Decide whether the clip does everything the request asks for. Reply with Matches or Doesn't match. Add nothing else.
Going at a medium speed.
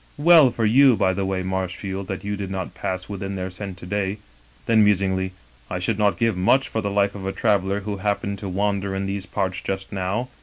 Doesn't match